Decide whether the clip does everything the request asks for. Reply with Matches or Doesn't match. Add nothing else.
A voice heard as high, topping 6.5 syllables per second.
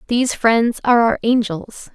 Doesn't match